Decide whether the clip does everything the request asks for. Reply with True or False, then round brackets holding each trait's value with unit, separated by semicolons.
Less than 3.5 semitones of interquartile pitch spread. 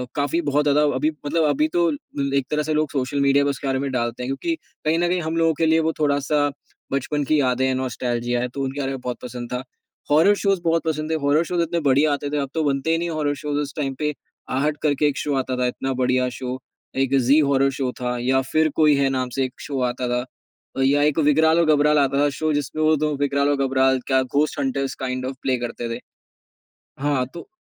True (2.6 semitones)